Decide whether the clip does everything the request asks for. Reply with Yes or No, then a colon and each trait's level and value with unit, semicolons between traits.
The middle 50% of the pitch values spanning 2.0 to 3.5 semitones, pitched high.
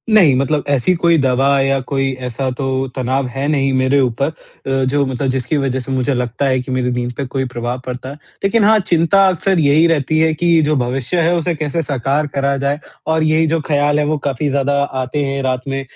No: average, 3.2 semitones; medium, 140 Hz